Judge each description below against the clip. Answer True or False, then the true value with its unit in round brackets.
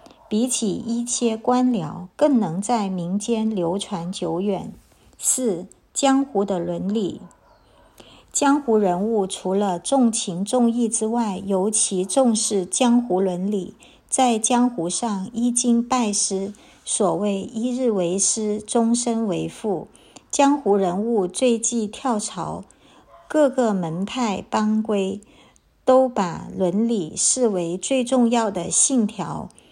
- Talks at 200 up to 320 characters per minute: False (170 characters per minute)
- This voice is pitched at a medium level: False (215 Hz)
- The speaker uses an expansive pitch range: False (3.9 semitones)